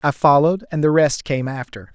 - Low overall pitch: No, medium, 145 Hz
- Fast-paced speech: Yes, fast, 215 wpm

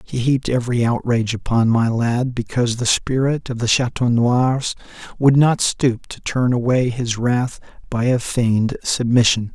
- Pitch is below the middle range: Yes, low, 120 Hz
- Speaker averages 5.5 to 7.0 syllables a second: No, 4.6 syllables/s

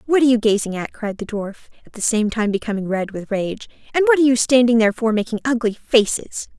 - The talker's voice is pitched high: Yes, high, 225 Hz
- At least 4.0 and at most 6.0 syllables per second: No, 6.3 syllables/s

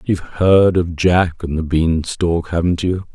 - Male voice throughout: Yes, male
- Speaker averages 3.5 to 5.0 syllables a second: Yes, 4.0 syllables/s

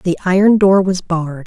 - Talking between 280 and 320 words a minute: No, fast, 205 wpm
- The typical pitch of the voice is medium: Yes, medium, 180 Hz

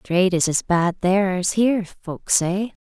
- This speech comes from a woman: Yes, female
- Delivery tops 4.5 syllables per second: No, 4.4 syllables/s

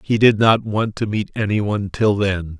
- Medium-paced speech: No, fast, 210 wpm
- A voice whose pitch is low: Yes, low, 105 Hz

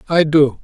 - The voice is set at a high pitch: No, medium, 150 Hz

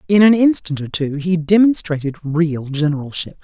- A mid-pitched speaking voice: Yes, medium, 165 Hz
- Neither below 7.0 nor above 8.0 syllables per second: No, 4.9 syllables/s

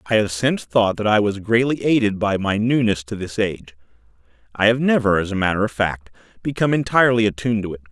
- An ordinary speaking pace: No, fast, 210 wpm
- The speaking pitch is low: Yes, low, 105 Hz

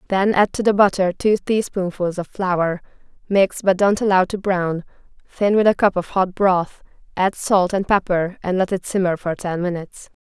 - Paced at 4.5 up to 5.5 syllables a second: Yes, 4.7 syllables/s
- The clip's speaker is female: Yes, female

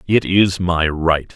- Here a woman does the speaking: No, male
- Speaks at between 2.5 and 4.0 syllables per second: Yes, 3.4 syllables/s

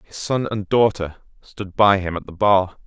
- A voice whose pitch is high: No, low, 100 Hz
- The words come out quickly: Yes, fast, 210 wpm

